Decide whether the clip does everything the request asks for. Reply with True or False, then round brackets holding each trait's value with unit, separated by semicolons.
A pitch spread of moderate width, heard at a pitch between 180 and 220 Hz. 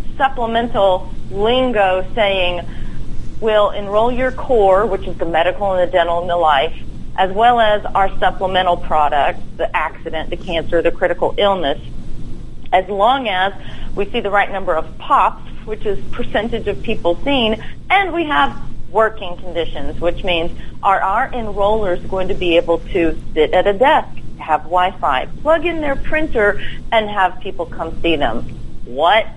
True (4.0 semitones; 190 Hz)